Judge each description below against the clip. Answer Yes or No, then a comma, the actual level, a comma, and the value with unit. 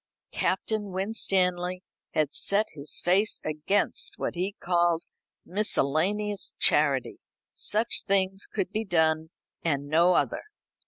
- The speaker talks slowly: Yes, slow, 110 wpm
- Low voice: No, medium, 185 Hz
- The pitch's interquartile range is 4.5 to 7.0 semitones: No, average, 4.0 semitones